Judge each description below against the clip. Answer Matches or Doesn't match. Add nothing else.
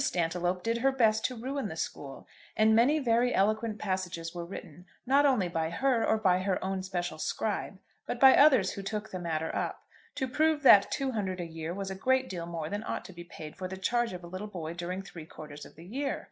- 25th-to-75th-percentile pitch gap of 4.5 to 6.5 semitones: Matches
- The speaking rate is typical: Doesn't match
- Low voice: Doesn't match